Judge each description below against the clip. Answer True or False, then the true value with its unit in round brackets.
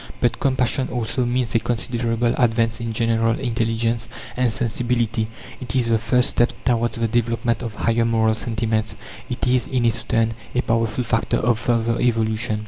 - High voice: False (115 Hz)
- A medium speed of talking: True (165 wpm)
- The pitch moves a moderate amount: False (1.2 semitones)